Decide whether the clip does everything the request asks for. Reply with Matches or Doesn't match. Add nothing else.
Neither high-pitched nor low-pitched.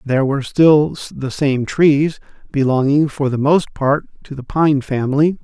Matches